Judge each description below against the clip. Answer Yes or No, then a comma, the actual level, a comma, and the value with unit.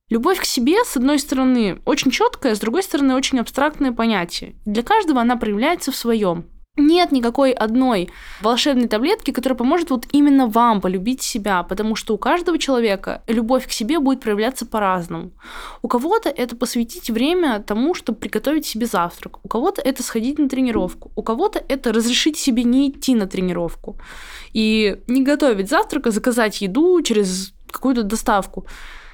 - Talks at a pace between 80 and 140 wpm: No, fast, 160 wpm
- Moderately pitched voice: No, high, 245 Hz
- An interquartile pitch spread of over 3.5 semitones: Yes, average, 4.5 semitones